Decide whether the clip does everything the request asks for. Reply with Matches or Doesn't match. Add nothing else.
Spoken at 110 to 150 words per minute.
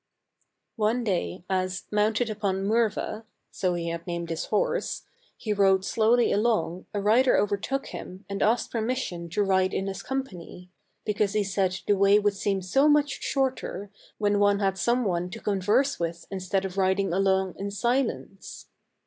Doesn't match